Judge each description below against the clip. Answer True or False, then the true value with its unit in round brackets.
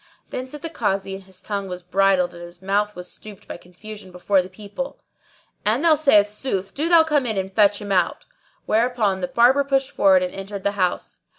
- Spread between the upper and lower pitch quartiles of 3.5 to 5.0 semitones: True (4.2 semitones)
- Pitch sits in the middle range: False (200 Hz)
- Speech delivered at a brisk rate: True (210 wpm)